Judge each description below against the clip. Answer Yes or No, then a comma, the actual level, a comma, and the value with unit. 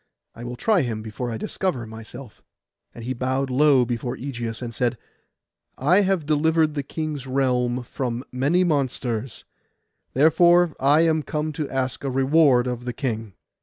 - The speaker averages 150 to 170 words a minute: Yes, average, 160 wpm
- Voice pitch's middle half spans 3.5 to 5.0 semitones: Yes, average, 3.9 semitones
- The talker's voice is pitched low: Yes, low, 130 Hz